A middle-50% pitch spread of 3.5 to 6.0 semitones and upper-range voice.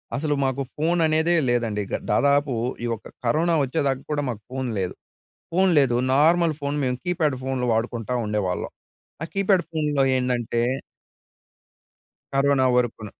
No: average, 4.3 semitones; low, 135 Hz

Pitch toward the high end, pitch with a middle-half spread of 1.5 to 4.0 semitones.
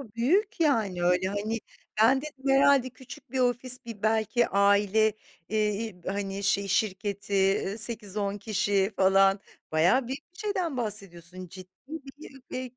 No: high, 215 Hz; average, 4.6 semitones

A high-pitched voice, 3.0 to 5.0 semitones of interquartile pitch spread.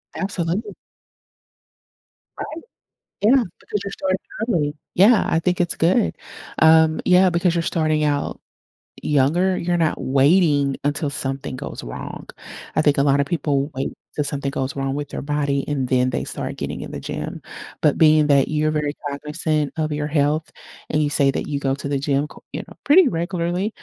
No: medium, 150 Hz; average, 3.3 semitones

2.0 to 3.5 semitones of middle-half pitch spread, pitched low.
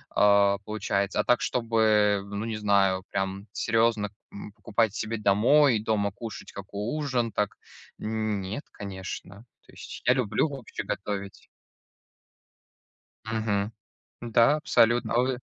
Yes: narrow, 2.4 semitones; low, 105 Hz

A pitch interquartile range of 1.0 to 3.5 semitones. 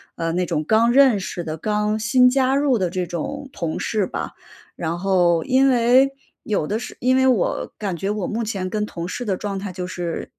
No: wide, 5.6 semitones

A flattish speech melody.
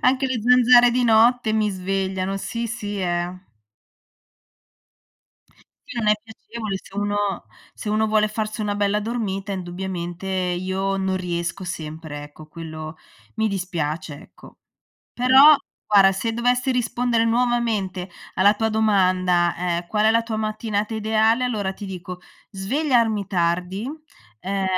No: average, 3.6 semitones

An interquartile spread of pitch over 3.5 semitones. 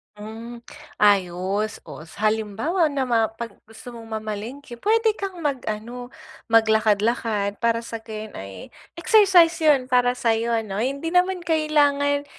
Yes: average, 5.0 semitones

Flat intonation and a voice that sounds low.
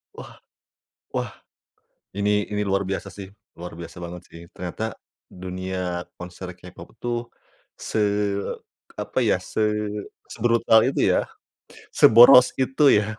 No: average, 3.8 semitones; low, 100 Hz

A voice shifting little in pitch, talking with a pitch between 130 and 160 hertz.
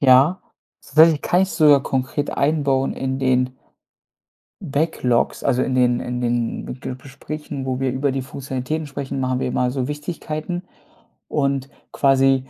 Yes: narrow, 2.3 semitones; low, 135 Hz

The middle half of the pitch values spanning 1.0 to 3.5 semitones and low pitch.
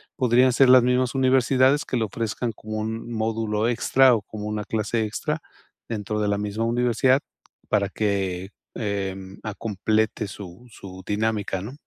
Yes: average, 2.8 semitones; low, 110 Hz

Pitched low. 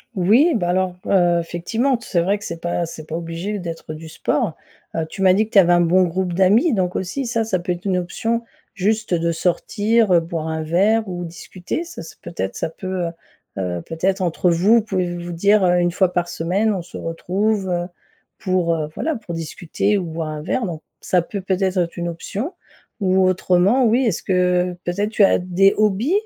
No: medium, 180 Hz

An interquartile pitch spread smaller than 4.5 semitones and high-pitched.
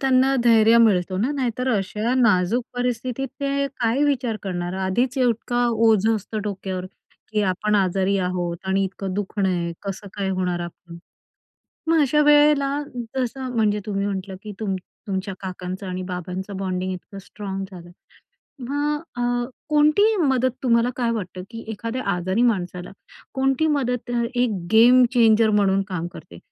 No: average, 4.9 semitones; high, 215 Hz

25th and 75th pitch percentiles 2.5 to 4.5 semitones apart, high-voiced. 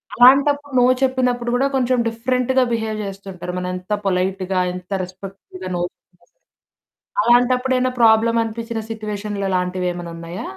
No: average, 5.0 semitones; high, 220 Hz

